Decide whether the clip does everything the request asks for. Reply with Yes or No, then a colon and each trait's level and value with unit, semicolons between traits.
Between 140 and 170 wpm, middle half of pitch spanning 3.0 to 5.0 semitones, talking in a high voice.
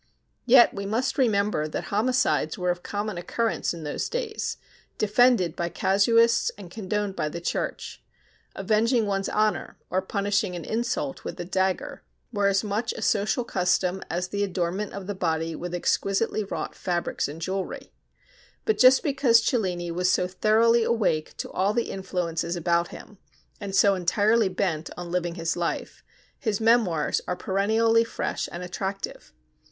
Yes: average, 160 wpm; average, 3.8 semitones; high, 195 Hz